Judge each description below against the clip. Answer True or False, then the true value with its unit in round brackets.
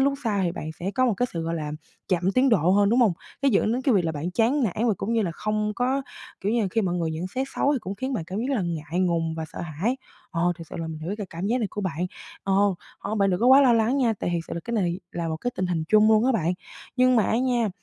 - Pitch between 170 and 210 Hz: True (200 Hz)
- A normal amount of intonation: False (5.7 semitones)